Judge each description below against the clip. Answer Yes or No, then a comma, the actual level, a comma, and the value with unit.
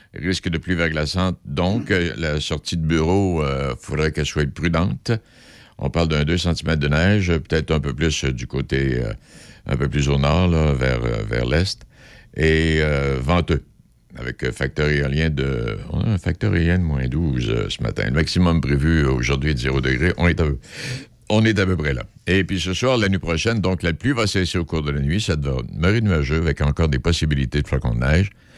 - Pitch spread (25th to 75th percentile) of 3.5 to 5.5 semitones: Yes, average, 4.2 semitones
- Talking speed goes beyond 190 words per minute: Yes, average, 215 wpm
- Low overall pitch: Yes, very low, 80 Hz